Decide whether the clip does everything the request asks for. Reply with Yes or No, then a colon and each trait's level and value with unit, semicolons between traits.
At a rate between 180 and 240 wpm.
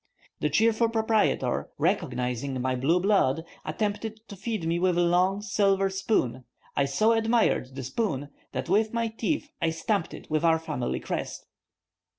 No: average, 160 wpm